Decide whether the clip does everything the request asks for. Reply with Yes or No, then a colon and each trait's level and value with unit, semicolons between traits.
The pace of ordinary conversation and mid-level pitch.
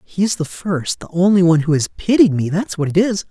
No: fast, 270 wpm; medium, 180 Hz